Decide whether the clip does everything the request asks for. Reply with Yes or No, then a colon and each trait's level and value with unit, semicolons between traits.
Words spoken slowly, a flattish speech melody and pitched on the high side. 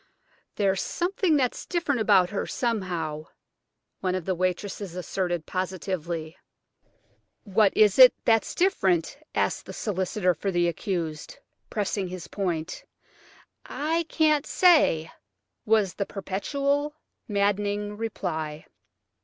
No: slow, 110 wpm; average, 4.3 semitones; high, 195 Hz